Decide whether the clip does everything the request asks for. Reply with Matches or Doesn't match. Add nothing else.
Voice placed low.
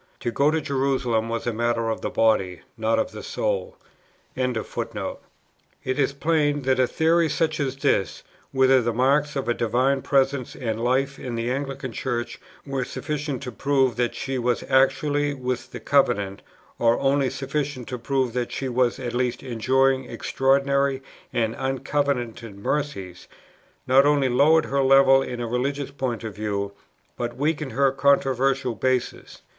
Matches